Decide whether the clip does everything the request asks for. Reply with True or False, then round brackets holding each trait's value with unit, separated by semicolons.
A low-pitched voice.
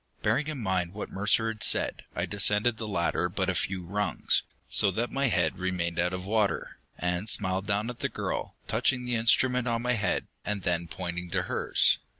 True (100 Hz)